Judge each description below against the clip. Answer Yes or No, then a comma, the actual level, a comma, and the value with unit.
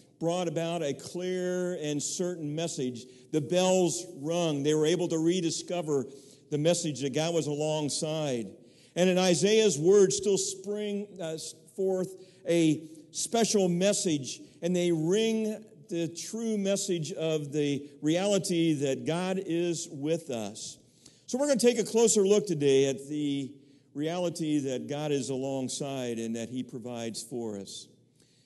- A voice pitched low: No, medium, 165 Hz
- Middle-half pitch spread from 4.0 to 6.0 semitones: Yes, average, 4.4 semitones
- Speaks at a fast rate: No, average, 140 wpm